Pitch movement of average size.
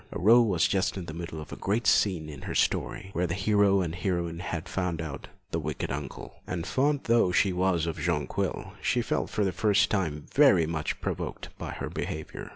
Yes: average, 3.5 semitones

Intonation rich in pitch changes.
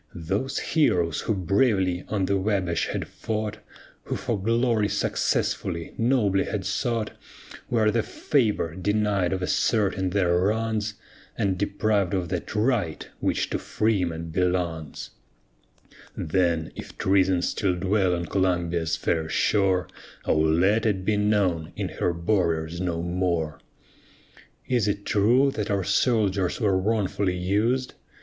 No: average, 3.3 semitones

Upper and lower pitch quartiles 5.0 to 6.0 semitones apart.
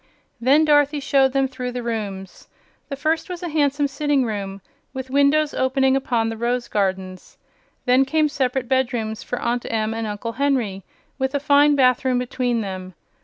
No: average, 3.9 semitones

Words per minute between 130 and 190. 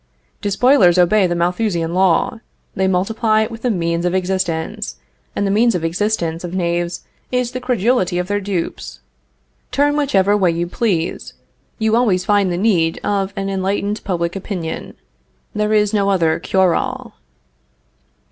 Yes: average, 150 wpm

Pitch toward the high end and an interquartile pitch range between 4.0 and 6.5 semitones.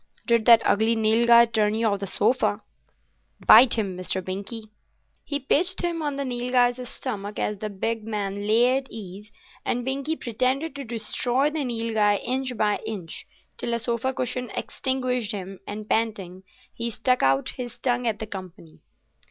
No: high, 230 Hz; average, 3.3 semitones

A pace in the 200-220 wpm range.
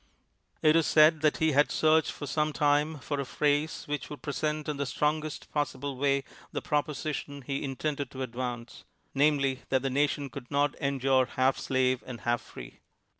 No: average, 185 wpm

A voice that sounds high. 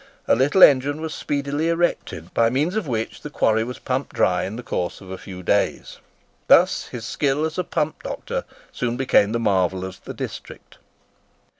No: low, 125 Hz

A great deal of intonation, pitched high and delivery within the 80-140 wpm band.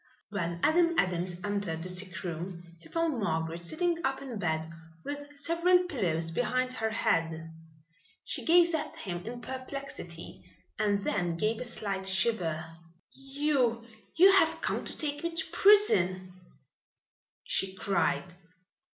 Yes: wide, 8.7 semitones; high, 215 Hz; slow, 135 wpm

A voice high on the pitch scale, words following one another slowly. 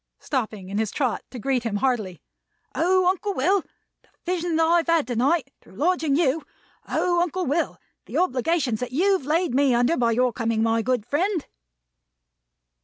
No: very high, 275 Hz; average, 175 wpm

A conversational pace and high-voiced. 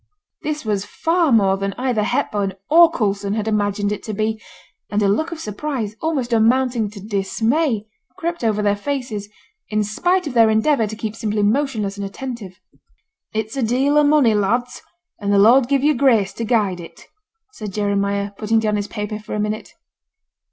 Yes: average, 180 wpm; high, 220 Hz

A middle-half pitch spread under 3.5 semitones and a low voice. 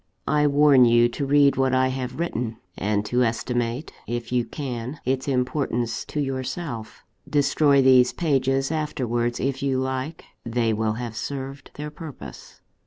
Yes: average, 2.8 semitones; low, 130 Hz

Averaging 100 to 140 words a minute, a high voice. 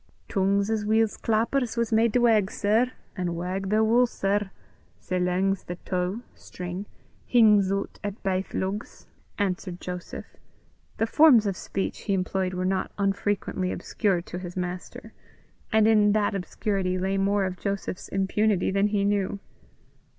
No: average, 160 wpm; high, 200 Hz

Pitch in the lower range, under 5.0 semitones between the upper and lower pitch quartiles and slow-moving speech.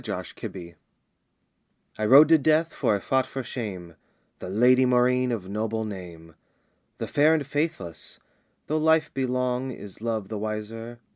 No: low, 120 Hz; average, 4.5 semitones; average, 165 wpm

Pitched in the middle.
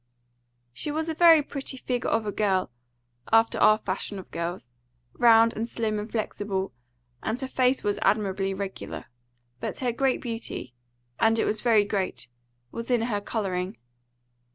No: high, 220 Hz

